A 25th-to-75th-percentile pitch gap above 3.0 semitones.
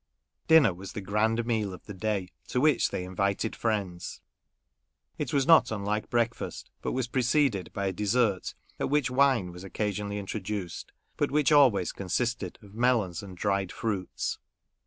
Yes: average, 4.1 semitones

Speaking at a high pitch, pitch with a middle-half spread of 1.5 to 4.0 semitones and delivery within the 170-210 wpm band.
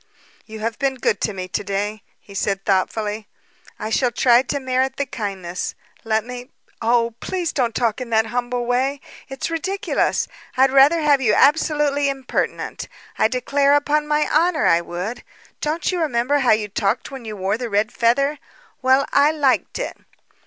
No: very high, 250 Hz; average, 4.6 semitones; average, 175 wpm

